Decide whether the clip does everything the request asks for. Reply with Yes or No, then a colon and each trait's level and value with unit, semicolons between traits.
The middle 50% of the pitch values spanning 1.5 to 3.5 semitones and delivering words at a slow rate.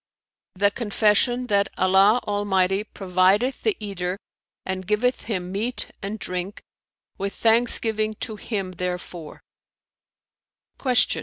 Yes: average, 2.8 semitones; slow, 100 wpm